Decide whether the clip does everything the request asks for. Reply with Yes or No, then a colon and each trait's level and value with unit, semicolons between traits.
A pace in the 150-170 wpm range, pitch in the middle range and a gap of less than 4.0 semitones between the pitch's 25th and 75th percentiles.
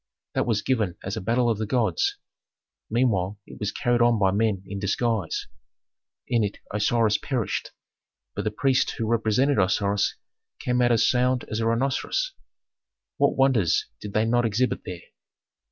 No: average, 160 wpm; low, 115 Hz; average, 3.2 semitones